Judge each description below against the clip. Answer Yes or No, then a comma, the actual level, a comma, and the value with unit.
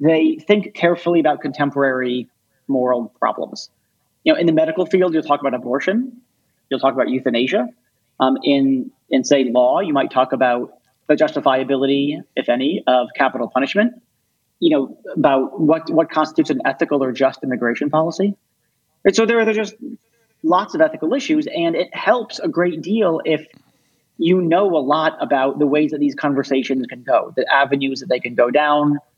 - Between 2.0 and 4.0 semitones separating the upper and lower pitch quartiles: No, wide, 5.5 semitones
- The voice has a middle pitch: Yes, medium, 145 Hz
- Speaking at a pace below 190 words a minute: Yes, average, 175 wpm